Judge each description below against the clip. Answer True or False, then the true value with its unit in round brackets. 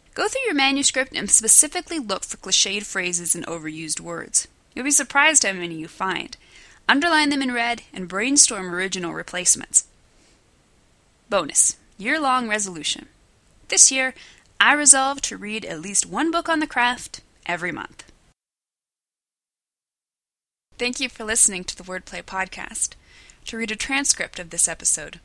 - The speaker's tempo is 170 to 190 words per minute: False (145 wpm)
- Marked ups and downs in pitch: True (6.9 semitones)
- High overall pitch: True (220 Hz)